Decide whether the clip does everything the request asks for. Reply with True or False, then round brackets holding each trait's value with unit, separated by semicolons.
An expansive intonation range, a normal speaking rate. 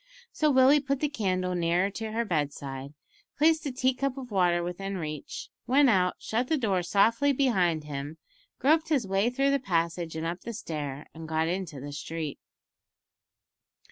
True (8.0 semitones; 175 wpm)